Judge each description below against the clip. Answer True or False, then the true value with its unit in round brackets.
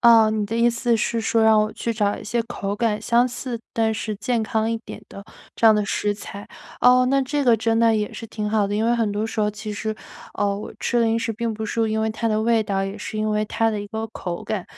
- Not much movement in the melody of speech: True (1.6 semitones)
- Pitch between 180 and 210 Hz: False (220 Hz)